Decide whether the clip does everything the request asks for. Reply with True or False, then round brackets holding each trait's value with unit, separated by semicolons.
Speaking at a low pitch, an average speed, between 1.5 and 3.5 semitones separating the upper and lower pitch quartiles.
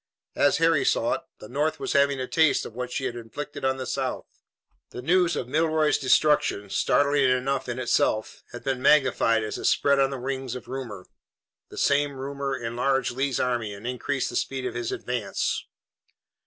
True (130 Hz; 185 wpm; 2.5 semitones)